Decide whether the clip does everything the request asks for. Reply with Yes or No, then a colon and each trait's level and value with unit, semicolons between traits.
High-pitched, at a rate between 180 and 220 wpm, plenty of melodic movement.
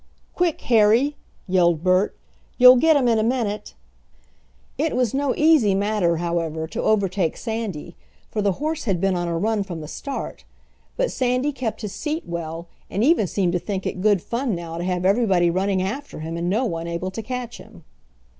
Yes: high, 200 Hz; average, 190 wpm; wide, 6.0 semitones